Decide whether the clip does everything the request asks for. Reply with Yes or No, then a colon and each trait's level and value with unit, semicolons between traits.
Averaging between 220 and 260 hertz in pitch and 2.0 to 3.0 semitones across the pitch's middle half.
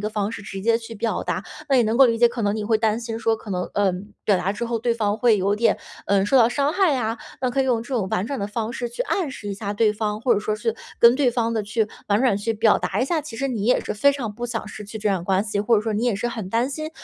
Yes: high, 225 Hz; narrow, 2.6 semitones